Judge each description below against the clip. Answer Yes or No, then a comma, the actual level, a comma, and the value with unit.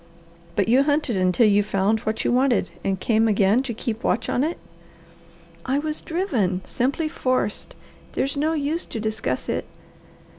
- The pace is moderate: Yes, average, 160 wpm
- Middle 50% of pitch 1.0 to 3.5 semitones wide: No, average, 5.1 semitones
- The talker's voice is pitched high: Yes, high, 235 Hz